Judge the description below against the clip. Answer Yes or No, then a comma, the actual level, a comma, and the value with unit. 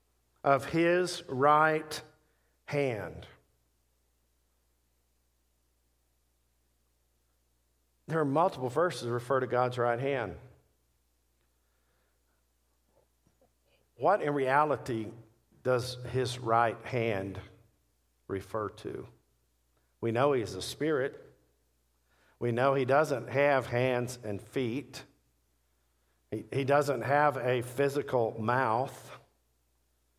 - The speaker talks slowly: Yes, slow, 85 wpm